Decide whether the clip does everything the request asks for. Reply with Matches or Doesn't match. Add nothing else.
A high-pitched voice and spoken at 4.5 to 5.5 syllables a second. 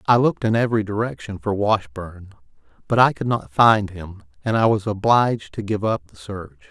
Doesn't match